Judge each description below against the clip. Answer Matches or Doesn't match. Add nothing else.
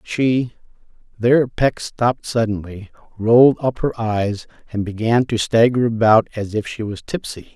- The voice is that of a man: Matches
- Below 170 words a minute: Matches